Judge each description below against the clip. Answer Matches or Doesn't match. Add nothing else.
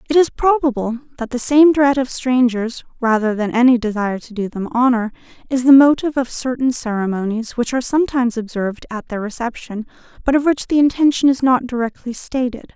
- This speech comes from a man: Doesn't match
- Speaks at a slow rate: Doesn't match